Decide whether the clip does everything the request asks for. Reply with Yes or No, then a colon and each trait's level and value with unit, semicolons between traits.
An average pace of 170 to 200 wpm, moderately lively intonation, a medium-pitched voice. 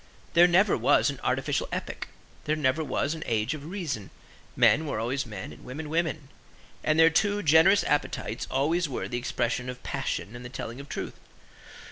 Yes: average, 180 wpm; average, 4.5 semitones; medium, 150 Hz